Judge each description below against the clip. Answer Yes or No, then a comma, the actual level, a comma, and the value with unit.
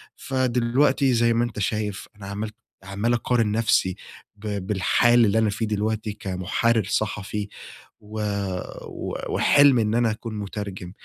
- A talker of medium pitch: No, low, 110 Hz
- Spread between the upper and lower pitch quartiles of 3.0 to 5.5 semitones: No, narrow, 2.5 semitones